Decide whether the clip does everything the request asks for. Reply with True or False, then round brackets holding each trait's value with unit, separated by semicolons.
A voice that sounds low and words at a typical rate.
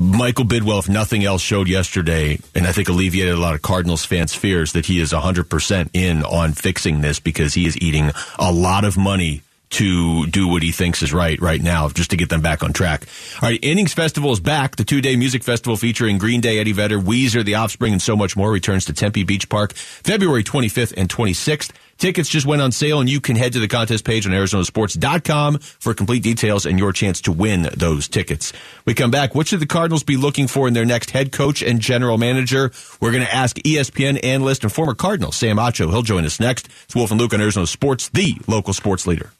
False (105 Hz; 230 wpm)